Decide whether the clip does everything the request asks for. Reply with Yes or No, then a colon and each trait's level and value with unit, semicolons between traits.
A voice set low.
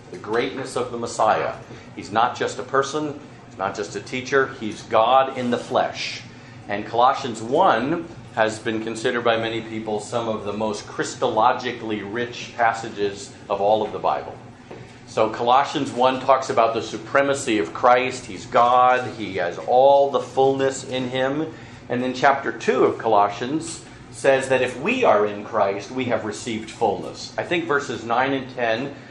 Yes: low, 120 Hz